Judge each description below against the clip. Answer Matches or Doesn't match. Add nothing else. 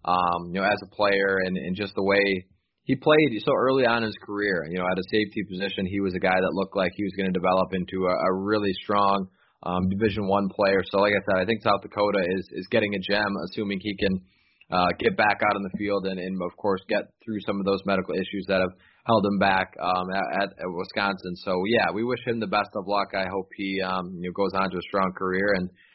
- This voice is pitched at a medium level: Doesn't match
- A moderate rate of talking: Doesn't match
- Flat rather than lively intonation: Matches